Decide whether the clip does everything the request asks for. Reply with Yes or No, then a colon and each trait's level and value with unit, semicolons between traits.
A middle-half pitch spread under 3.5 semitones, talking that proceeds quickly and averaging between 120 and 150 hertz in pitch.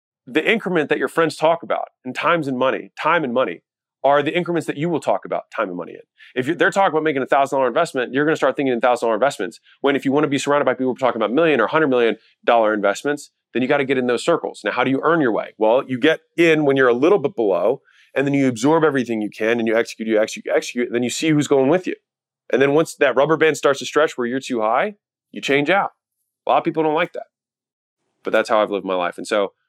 No: average, 4.0 semitones; fast, 280 wpm; medium, 140 Hz